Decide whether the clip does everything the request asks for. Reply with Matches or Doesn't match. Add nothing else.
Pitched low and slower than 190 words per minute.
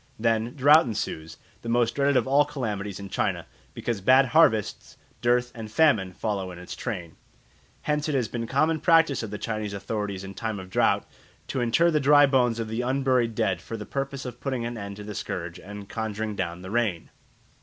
Doesn't match